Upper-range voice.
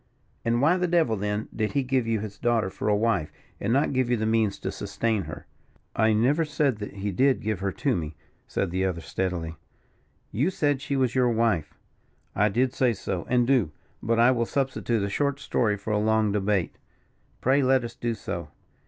No: low, 115 Hz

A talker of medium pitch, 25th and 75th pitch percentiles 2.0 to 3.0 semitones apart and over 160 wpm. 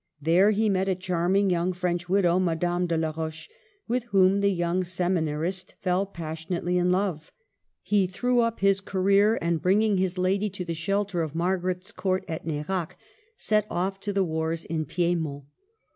Yes: medium, 180 Hz; narrow, 2.6 semitones; average, 170 wpm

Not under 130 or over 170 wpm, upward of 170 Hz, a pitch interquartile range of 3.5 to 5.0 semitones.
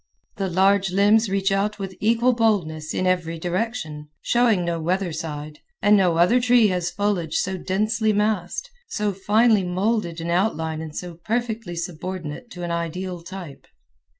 Yes: average, 155 wpm; high, 190 Hz; average, 3.9 semitones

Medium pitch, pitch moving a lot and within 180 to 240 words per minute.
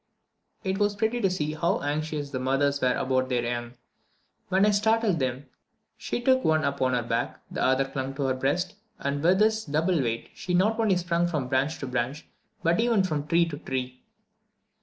Yes: medium, 150 Hz; wide, 6.1 semitones; average, 200 wpm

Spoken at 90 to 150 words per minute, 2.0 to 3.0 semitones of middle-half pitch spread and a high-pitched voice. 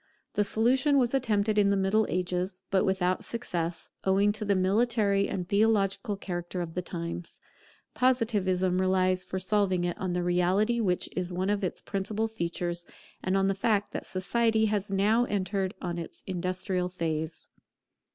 No: average, 160 wpm; narrow, 2.6 semitones; high, 195 Hz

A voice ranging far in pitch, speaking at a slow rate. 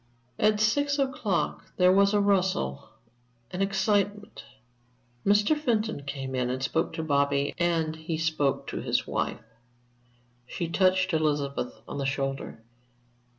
Yes: wide, 6.3 semitones; slow, 130 wpm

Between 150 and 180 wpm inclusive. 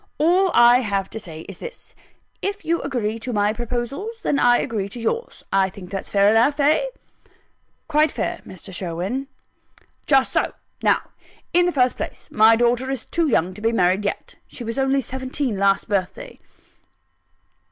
Yes: average, 170 wpm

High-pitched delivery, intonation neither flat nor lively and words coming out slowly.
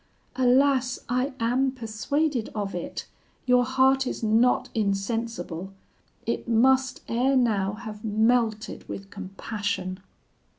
Yes: high, 230 Hz; average, 3.7 semitones; slow, 110 wpm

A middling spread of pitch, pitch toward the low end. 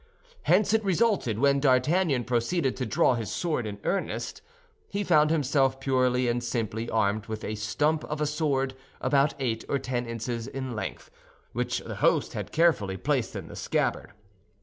Yes: average, 4.5 semitones; low, 130 Hz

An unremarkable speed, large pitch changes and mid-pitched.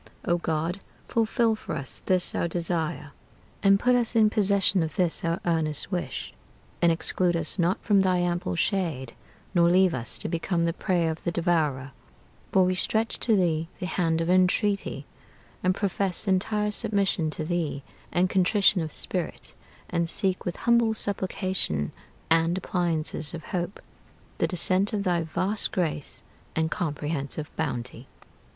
No: average, 155 wpm; average, 3.0 semitones; medium, 175 Hz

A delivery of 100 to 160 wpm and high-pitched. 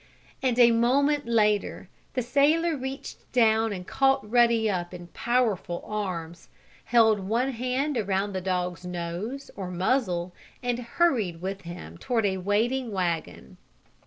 Yes: slow, 135 wpm; high, 220 Hz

